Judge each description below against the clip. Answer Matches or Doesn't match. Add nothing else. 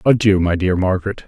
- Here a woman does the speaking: Doesn't match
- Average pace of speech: Matches